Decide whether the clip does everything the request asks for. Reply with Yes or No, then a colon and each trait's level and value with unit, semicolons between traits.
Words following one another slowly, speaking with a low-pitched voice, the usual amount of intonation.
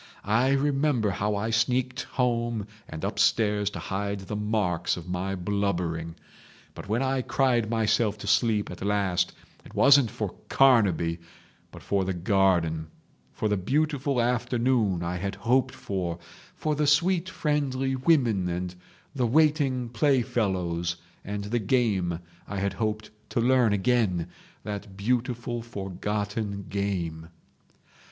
Yes: slow, 130 wpm; low, 105 Hz; average, 4.6 semitones